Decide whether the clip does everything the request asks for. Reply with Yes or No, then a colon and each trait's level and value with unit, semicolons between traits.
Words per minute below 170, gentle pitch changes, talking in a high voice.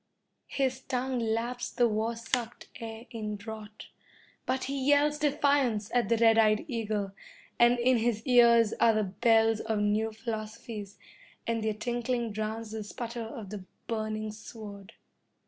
Yes: average, 145 wpm; narrow, 2.0 semitones; high, 225 Hz